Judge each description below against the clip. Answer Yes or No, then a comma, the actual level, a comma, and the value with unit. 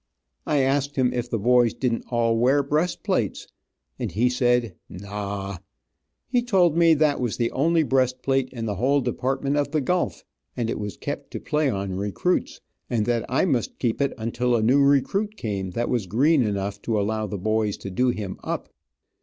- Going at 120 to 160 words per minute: No, average, 195 wpm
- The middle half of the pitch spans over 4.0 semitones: Yes, average, 4.5 semitones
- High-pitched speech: No, low, 125 Hz